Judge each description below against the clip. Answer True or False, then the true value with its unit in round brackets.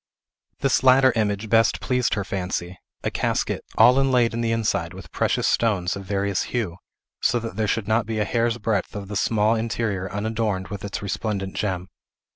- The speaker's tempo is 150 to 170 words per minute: False (185 wpm)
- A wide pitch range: False (2.8 semitones)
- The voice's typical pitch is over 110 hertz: False (105 Hz)